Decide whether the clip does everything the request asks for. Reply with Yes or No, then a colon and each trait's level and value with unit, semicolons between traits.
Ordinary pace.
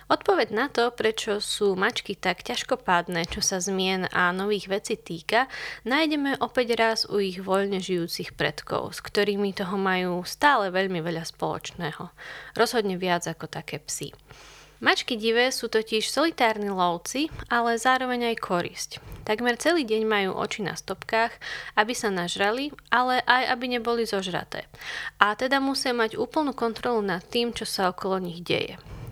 Yes: average, 150 wpm